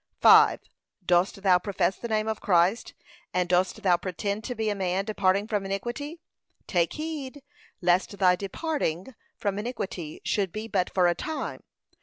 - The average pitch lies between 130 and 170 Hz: No, high, 200 Hz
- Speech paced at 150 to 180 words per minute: Yes, average, 160 wpm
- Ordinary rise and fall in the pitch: Yes, average, 3.5 semitones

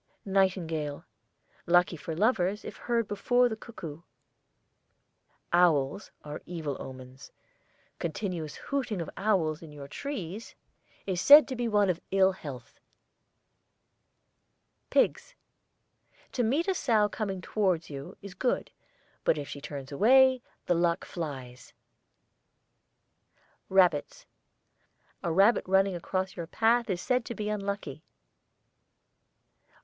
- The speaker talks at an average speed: No, slow, 115 wpm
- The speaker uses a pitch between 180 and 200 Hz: Yes, medium, 185 Hz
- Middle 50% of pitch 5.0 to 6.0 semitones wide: Yes, average, 5.3 semitones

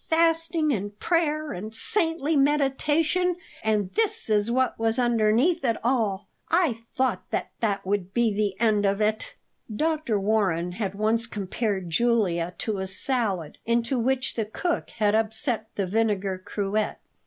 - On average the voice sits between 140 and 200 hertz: No, high, 225 Hz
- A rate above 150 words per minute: No, average, 140 wpm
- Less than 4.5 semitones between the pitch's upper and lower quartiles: No, average, 5.0 semitones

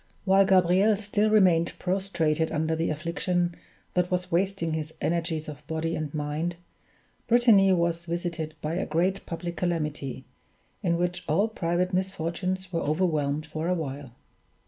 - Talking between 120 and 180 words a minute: Yes, average, 145 wpm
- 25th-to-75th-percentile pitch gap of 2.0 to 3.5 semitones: Yes, average, 2.8 semitones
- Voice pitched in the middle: Yes, medium, 170 Hz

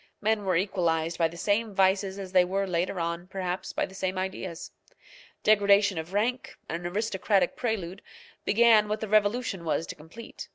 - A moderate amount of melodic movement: Yes, average, 3.0 semitones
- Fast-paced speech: No, average, 170 wpm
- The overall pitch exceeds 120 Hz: Yes, high, 190 Hz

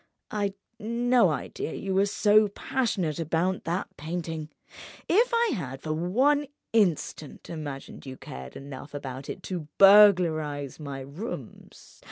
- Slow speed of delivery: Yes, slow, 130 wpm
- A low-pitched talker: No, medium, 170 Hz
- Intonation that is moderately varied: No, wide, 6.1 semitones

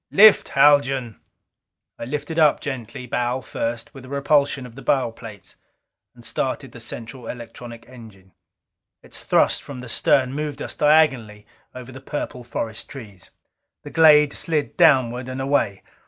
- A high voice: No, low, 130 Hz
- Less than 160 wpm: Yes, average, 150 wpm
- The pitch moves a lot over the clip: No, average, 3.5 semitones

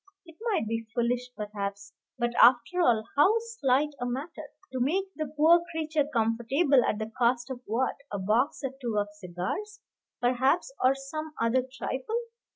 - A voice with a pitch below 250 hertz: No, very high, 255 Hz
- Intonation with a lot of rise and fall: No, average, 4.9 semitones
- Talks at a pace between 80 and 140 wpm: No, average, 165 wpm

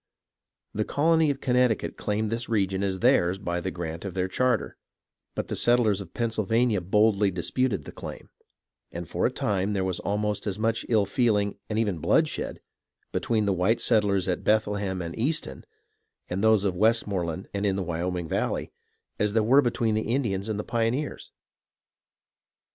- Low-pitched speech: Yes, low, 105 Hz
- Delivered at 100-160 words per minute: No, average, 170 wpm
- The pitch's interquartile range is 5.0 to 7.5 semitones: No, average, 3.2 semitones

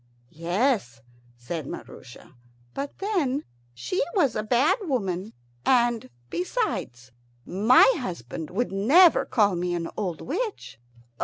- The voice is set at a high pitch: Yes, high, 215 Hz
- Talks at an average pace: No, slow, 110 wpm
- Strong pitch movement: Yes, wide, 8.2 semitones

